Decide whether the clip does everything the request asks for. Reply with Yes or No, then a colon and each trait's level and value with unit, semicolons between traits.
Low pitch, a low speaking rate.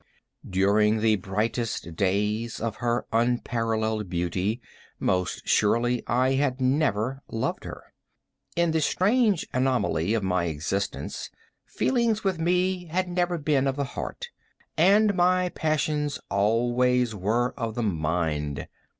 Yes: low, 120 Hz; slow, 125 wpm